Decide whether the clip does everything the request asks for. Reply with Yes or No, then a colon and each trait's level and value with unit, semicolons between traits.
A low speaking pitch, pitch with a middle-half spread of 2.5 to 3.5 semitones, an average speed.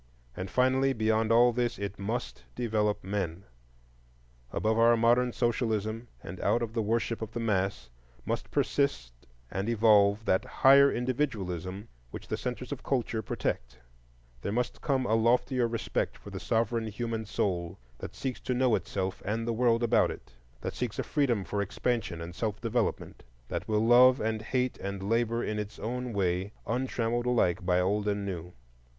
Yes: low, 110 Hz; average, 3.2 semitones; average, 170 wpm